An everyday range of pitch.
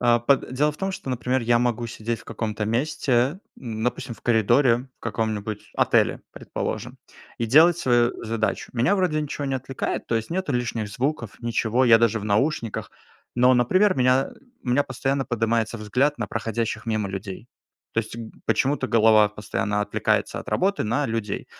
Yes: average, 3.2 semitones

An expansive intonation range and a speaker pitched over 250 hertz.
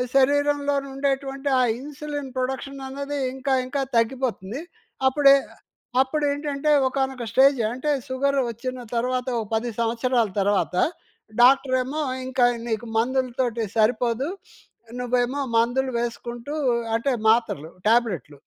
No: average, 2.7 semitones; very high, 260 Hz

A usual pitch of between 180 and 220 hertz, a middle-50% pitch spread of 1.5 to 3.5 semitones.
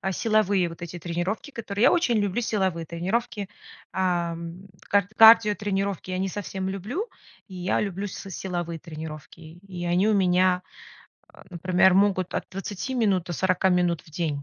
Yes: medium, 185 Hz; average, 2.7 semitones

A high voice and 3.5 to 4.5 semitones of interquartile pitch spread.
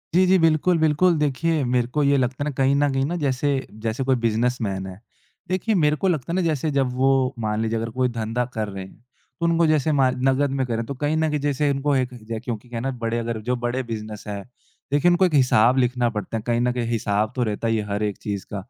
No: low, 130 Hz; average, 4.2 semitones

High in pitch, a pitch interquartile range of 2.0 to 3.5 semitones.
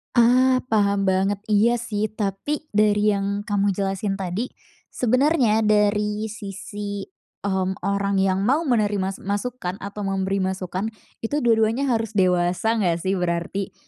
Yes: high, 205 Hz; narrow, 2.4 semitones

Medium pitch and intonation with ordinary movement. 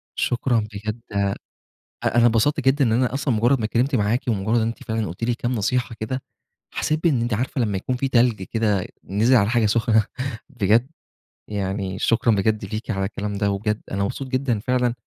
No: low, 115 Hz; average, 3.2 semitones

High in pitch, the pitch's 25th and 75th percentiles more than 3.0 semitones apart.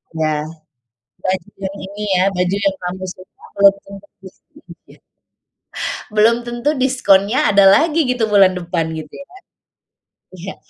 Yes: high, 195 Hz; average, 3.6 semitones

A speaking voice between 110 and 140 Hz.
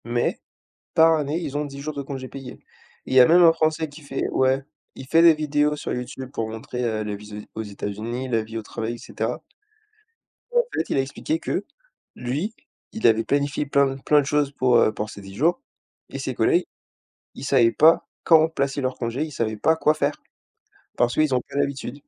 Yes: low, 135 Hz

